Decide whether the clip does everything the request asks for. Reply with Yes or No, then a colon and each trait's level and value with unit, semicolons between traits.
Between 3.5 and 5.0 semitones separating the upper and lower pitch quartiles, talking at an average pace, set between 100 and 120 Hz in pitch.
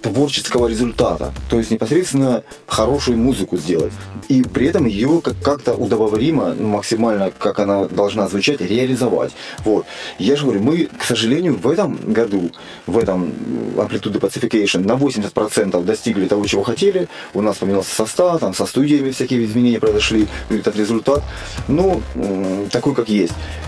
Yes: average, 4.1 semitones; average, 140 wpm; low, 110 Hz